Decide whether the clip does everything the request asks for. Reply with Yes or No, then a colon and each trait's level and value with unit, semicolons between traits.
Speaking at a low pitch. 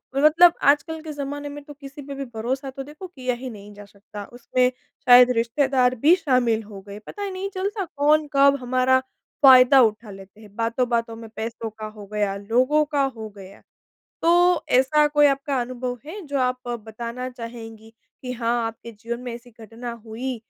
No: very high, 250 Hz